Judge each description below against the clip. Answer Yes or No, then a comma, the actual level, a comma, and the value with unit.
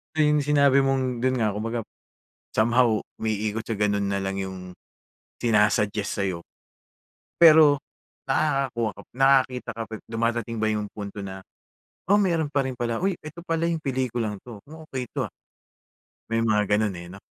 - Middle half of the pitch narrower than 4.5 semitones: No, average, 4.8 semitones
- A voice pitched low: Yes, low, 120 Hz